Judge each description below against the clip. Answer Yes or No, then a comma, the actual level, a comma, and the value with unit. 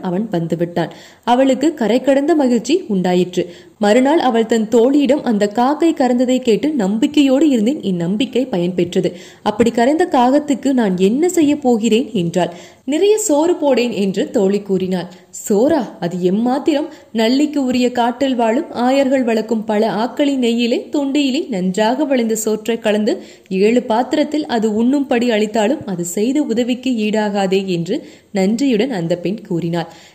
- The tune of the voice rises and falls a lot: Yes, wide, 5.8 semitones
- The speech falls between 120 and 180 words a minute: Yes, average, 125 wpm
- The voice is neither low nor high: No, high, 235 Hz